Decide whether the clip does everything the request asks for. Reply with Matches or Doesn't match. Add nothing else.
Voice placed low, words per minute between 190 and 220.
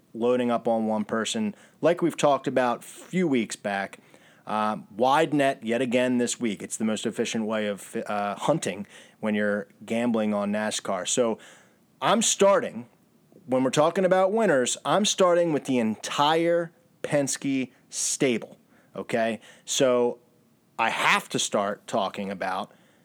Doesn't match